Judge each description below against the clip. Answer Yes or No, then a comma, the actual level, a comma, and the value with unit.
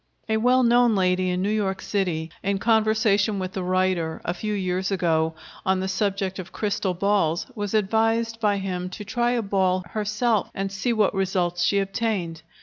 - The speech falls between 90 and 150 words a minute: No, average, 180 wpm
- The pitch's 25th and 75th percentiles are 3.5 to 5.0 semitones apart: No, average, 2.8 semitones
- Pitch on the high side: Yes, high, 195 Hz